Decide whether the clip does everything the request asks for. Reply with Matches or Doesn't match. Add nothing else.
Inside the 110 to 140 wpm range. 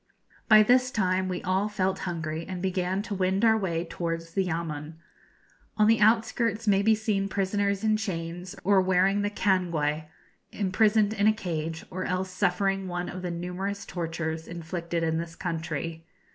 Doesn't match